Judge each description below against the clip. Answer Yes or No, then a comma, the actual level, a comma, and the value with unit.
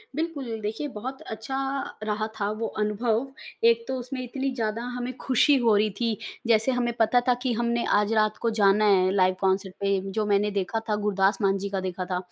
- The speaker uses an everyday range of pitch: Yes, average, 3.3 semitones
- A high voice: Yes, high, 215 Hz